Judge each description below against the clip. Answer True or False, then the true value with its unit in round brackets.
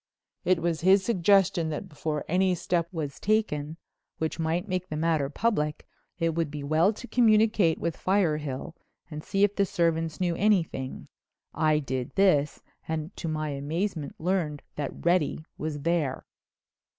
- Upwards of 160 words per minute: False (150 wpm)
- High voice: False (165 Hz)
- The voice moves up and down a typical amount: True (3.7 semitones)